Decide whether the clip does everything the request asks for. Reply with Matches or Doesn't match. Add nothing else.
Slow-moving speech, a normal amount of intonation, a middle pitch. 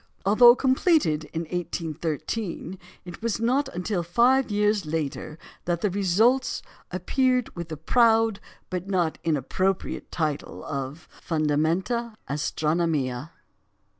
Doesn't match